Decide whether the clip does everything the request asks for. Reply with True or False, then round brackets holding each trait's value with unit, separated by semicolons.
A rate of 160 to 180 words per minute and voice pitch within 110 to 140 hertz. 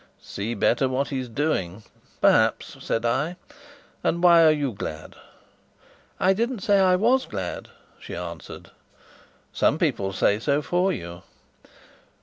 False (135 wpm; 135 Hz)